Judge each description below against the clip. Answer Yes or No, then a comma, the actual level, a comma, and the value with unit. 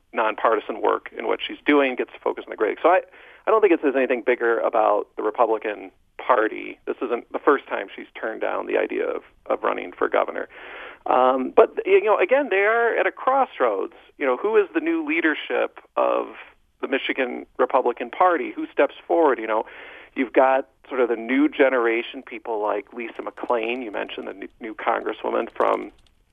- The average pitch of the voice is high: Yes, very high, 305 Hz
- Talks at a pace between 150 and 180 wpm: No, average, 195 wpm